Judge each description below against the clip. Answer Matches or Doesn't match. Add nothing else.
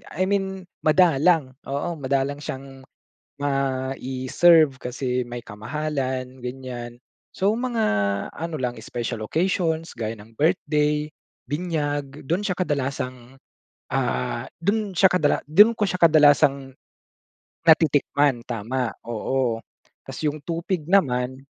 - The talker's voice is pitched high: Doesn't match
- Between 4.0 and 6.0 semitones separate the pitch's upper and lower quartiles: Matches